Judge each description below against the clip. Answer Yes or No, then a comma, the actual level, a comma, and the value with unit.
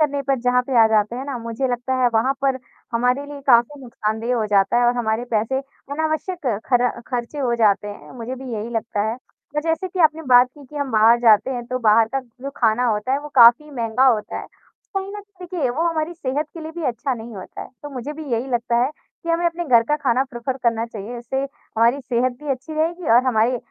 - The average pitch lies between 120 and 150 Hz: No, very high, 250 Hz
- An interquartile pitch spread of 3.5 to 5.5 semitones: Yes, average, 3.9 semitones